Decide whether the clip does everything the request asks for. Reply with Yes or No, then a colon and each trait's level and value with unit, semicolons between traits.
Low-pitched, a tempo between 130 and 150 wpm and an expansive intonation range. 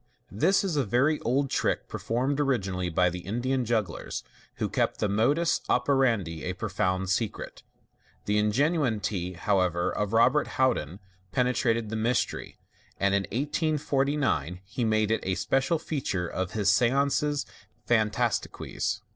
Yes: low, 115 Hz; average, 140 wpm; wide, 5.8 semitones